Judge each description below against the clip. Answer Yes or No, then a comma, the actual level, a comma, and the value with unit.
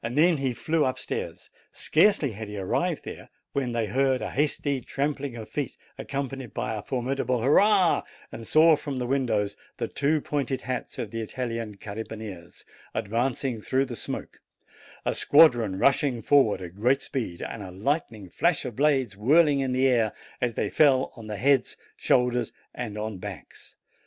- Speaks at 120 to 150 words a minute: No, average, 165 wpm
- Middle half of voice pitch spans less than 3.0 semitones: No, average, 4.0 semitones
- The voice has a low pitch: Yes, low, 125 Hz